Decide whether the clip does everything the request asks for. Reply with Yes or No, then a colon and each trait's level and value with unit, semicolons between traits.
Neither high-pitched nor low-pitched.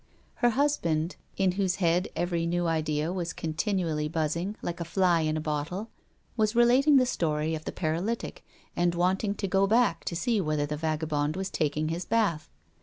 Yes: medium, 175 Hz